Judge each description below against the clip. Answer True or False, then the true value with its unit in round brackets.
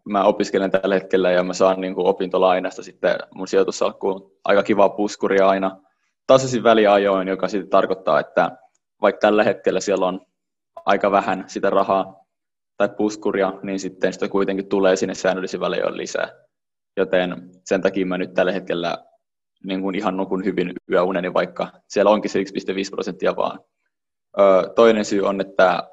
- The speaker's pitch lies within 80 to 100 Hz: True (95 Hz)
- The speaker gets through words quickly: True (160 wpm)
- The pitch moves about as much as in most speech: False (1.1 semitones)